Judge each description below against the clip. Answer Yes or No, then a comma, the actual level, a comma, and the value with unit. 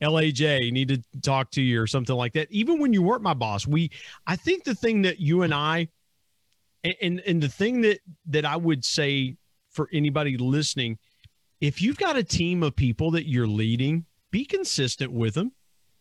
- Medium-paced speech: Yes, average, 190 wpm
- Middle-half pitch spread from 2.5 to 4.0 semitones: No, average, 5.3 semitones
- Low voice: No, medium, 150 Hz